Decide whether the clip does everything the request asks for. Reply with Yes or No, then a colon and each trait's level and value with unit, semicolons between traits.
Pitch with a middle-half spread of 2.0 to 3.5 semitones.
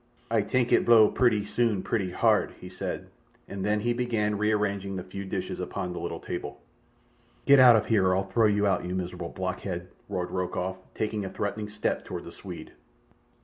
Yes: average, 2.7 semitones